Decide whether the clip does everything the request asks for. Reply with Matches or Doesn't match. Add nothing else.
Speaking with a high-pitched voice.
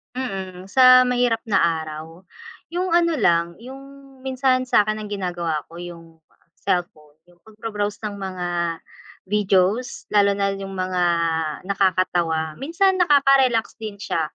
Matches